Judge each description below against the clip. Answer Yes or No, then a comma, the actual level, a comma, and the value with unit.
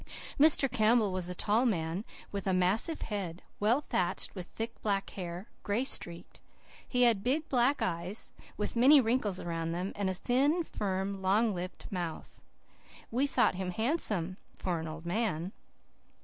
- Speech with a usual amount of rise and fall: Yes, average, 4.9 semitones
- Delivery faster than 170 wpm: No, average, 160 wpm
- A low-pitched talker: No, high, 200 Hz